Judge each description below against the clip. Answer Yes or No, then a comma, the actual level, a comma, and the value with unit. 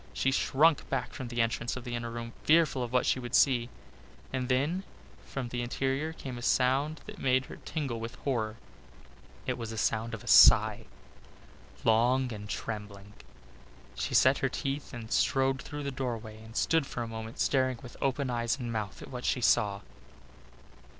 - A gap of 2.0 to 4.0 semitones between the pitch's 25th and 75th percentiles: Yes, average, 2.8 semitones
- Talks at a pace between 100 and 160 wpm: No, average, 185 wpm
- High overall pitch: No, low, 125 Hz